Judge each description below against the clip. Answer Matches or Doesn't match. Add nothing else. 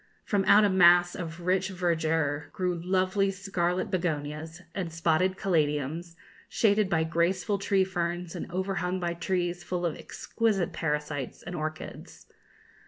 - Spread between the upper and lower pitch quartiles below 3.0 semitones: Matches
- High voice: Doesn't match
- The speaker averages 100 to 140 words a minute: Matches